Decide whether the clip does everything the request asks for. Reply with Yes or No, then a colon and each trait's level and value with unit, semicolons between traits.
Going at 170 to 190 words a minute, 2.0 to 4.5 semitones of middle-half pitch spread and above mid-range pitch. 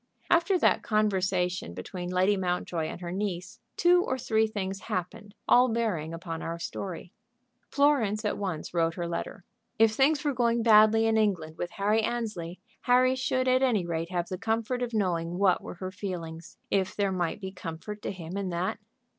Yes: average, 180 wpm; average, 4.2 semitones; high, 195 Hz